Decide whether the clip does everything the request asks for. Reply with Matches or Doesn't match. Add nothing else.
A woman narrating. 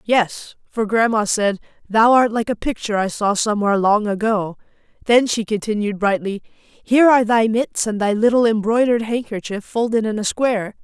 Matches